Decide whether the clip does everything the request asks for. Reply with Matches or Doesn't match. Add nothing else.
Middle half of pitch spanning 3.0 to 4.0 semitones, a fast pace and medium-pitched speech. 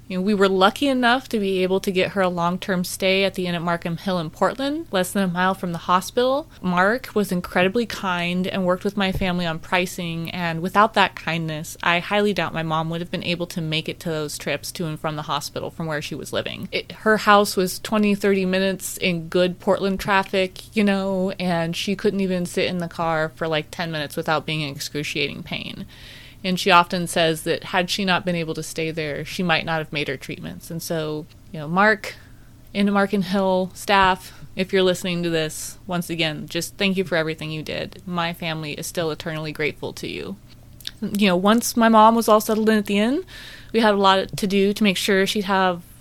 Matches